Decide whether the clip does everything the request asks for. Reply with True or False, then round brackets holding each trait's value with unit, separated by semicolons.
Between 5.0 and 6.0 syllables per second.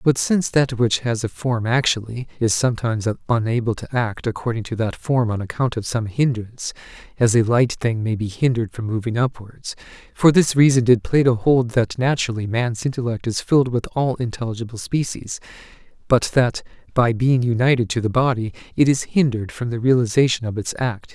True (5.5 syllables/s)